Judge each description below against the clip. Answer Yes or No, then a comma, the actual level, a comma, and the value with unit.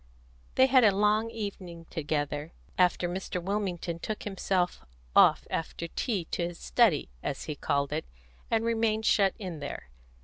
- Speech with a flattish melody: No, average, 4.5 semitones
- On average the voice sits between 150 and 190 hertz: Yes, medium, 185 Hz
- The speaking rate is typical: Yes, average, 150 wpm